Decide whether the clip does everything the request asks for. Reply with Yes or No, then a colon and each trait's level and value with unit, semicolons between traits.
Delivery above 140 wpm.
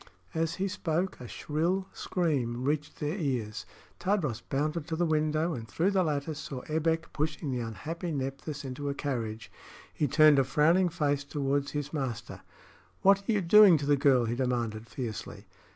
Yes: average, 170 wpm